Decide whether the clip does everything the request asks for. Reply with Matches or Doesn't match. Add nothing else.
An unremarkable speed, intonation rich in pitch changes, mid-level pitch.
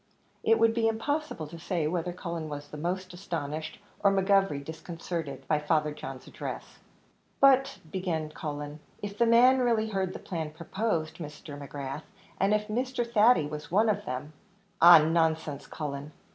Matches